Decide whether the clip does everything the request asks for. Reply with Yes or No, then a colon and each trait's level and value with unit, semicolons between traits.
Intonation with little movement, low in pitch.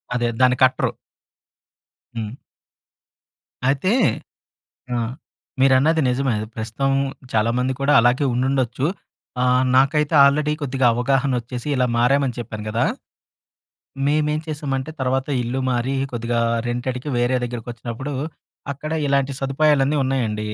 Yes: narrow, 2.3 semitones; low, 130 Hz